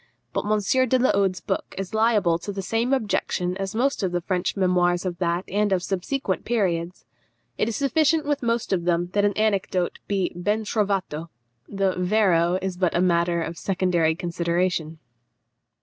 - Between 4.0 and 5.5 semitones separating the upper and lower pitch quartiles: No, average, 3.3 semitones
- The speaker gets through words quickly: No, average, 170 wpm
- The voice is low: No, high, 190 Hz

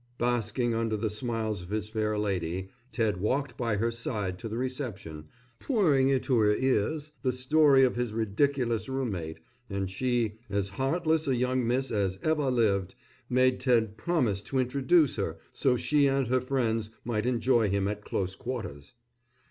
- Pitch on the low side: Yes, low, 115 Hz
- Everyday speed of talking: Yes, average, 165 wpm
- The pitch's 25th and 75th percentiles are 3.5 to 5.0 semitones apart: Yes, average, 3.9 semitones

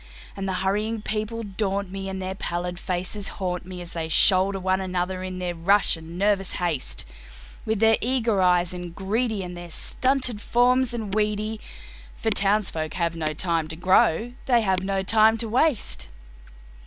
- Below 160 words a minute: No, average, 170 wpm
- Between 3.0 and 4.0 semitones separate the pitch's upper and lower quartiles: Yes, average, 3.3 semitones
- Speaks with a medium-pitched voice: No, high, 195 Hz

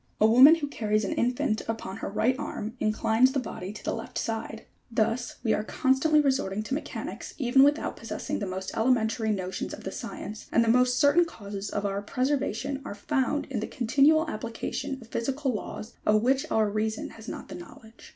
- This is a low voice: No, high, 230 Hz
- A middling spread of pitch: Yes, average, 3.9 semitones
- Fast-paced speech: No, average, 195 wpm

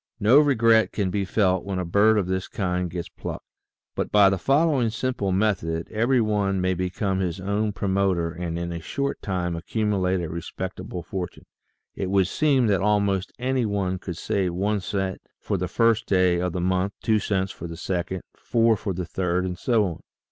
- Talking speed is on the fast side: No, average, 190 wpm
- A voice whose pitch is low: Yes, very low, 95 Hz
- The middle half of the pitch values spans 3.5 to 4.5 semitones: No, average, 2.9 semitones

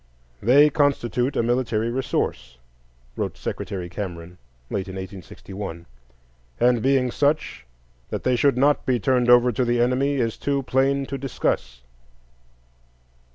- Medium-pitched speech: No, low, 125 Hz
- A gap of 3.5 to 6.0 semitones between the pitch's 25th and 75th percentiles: Yes, average, 5.2 semitones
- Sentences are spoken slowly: Yes, slow, 130 wpm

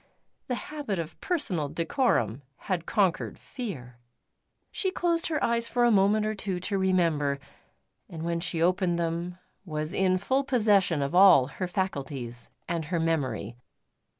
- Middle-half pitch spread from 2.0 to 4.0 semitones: No, average, 5.2 semitones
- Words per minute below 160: Yes, average, 150 wpm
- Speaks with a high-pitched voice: No, medium, 180 Hz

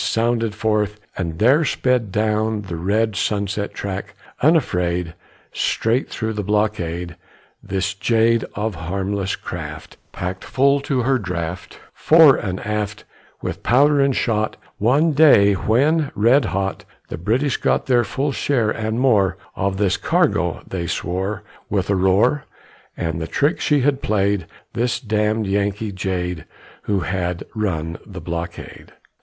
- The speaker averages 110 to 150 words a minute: Yes, average, 140 wpm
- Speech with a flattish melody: No, average, 4.3 semitones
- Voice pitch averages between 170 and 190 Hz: No, low, 105 Hz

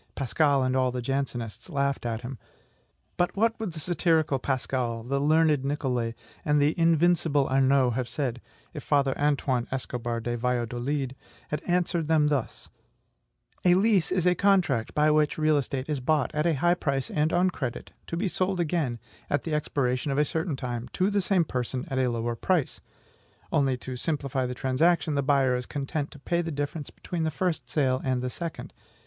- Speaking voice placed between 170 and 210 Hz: No, medium, 140 Hz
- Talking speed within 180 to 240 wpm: Yes, average, 185 wpm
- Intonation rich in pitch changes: No, average, 4.1 semitones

